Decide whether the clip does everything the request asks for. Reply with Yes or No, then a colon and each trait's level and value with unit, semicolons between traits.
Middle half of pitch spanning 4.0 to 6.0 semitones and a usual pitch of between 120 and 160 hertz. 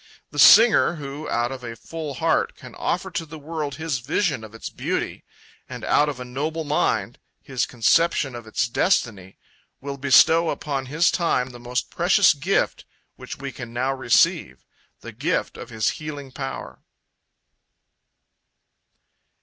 Yes: average, 4.3 semitones; medium, 140 Hz